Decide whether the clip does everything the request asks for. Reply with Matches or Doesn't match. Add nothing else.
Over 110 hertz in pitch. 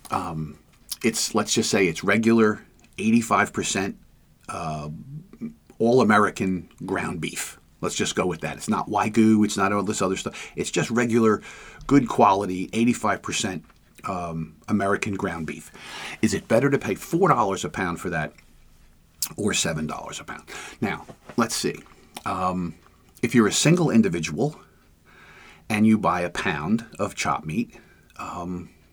Doesn't match